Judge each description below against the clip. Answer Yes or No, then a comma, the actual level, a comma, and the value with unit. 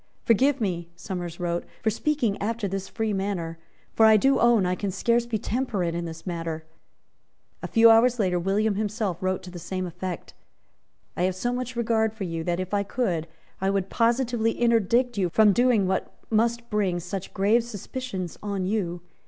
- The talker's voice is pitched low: No, high, 200 Hz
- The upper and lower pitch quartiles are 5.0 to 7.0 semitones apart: No, average, 4.2 semitones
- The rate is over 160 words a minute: Yes, average, 185 wpm